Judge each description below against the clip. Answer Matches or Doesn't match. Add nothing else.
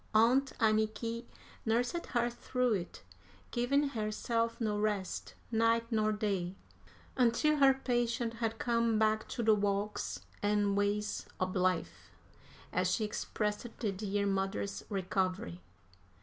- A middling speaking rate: Doesn't match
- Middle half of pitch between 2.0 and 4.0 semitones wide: Matches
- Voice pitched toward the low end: Doesn't match